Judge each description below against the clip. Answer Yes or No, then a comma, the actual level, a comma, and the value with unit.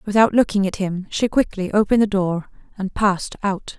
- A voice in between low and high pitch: No, high, 200 Hz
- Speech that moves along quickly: No, average, 190 wpm